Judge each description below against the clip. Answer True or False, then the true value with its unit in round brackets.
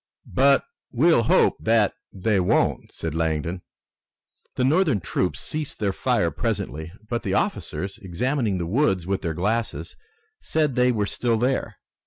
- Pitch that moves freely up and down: True (5.8 semitones)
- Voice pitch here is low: True (110 Hz)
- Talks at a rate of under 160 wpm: True (145 wpm)